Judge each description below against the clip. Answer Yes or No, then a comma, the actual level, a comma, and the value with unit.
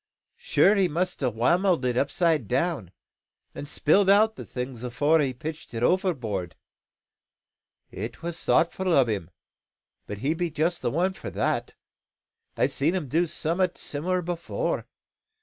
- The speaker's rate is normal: Yes, average, 150 wpm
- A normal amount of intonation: No, wide, 6.1 semitones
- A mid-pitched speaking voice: Yes, medium, 160 Hz